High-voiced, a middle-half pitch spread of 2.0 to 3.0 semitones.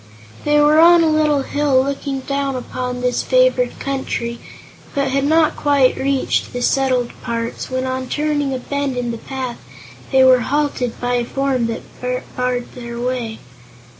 Yes: very high, 265 Hz; narrow, 2.4 semitones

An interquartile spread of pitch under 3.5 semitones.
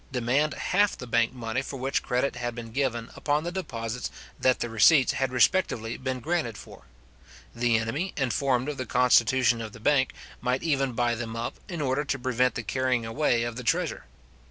Yes: average, 2.7 semitones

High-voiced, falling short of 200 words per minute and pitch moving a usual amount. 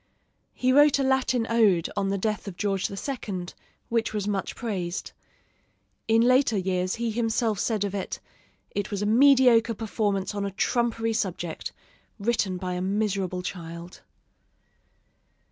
Yes: high, 210 Hz; average, 145 wpm; average, 3.4 semitones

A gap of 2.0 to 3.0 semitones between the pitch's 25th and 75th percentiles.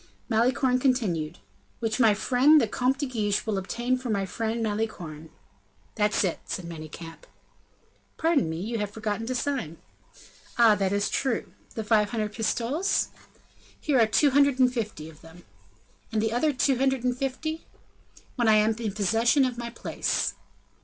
No: average, 3.7 semitones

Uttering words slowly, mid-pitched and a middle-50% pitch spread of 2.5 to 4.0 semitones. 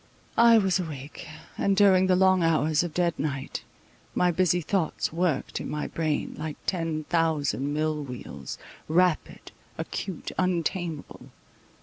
Yes: slow, 130 wpm; medium, 165 Hz; average, 3.2 semitones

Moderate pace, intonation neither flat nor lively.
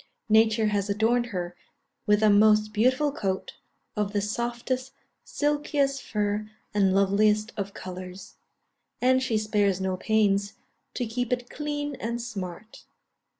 No: slow, 130 wpm; average, 3.3 semitones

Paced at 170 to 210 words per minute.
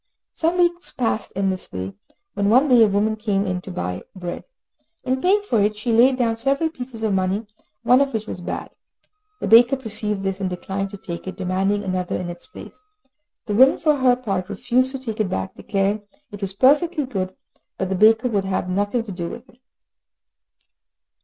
Yes: average, 200 wpm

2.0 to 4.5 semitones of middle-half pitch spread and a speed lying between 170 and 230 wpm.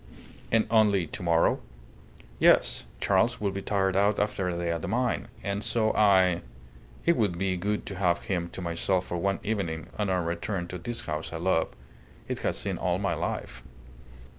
Yes: average, 3.2 semitones; average, 190 wpm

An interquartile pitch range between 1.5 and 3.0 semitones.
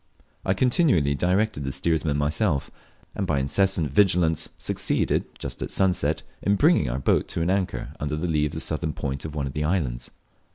No: average, 4.7 semitones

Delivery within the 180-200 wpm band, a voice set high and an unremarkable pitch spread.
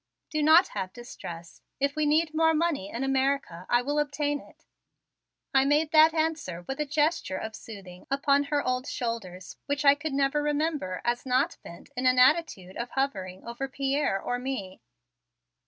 No: average, 170 wpm; very high, 275 Hz; average, 4.3 semitones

